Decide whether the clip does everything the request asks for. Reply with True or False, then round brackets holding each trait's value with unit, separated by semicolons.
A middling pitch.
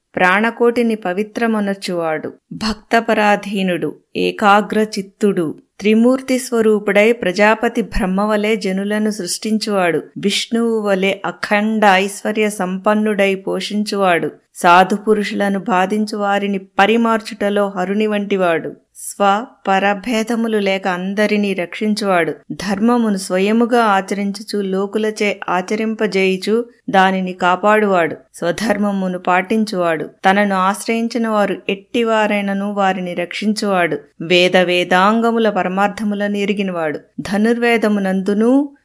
False (205 Hz)